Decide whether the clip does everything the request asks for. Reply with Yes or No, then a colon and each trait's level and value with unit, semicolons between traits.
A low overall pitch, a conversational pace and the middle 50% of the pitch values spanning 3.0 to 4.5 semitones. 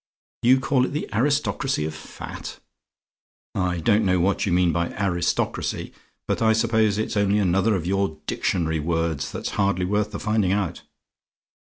Yes: low, 100 Hz; average, 160 wpm; average, 3.9 semitones